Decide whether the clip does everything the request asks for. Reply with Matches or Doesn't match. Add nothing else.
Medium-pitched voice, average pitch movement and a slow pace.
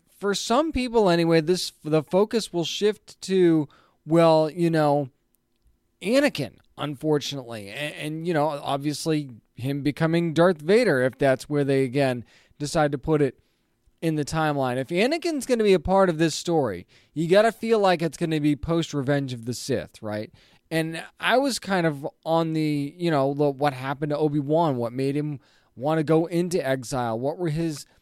Doesn't match